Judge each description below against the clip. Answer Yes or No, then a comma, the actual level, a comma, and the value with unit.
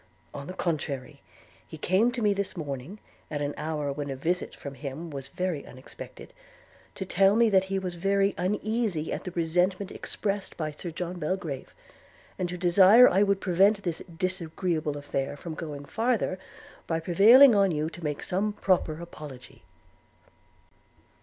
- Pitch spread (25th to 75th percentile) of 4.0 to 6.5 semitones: Yes, average, 4.5 semitones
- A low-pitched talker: No, medium, 175 Hz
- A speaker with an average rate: Yes, average, 160 wpm